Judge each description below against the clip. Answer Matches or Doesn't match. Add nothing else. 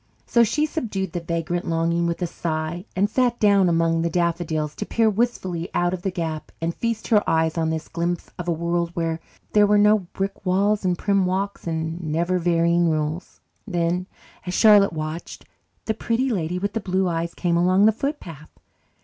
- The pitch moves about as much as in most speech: Matches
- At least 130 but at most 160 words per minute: Doesn't match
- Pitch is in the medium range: Matches